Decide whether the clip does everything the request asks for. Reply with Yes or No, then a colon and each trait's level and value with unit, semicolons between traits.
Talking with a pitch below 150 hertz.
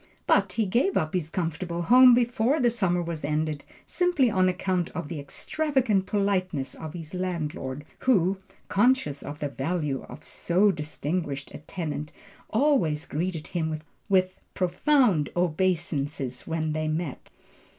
No: medium, 175 Hz